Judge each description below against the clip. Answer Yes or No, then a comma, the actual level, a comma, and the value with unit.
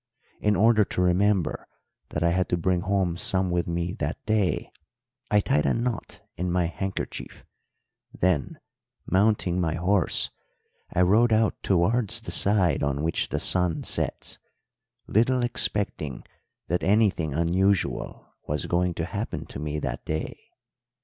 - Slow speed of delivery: No, average, 145 wpm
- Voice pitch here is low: Yes, very low, 90 Hz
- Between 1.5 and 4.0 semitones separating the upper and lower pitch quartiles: Yes, average, 3.4 semitones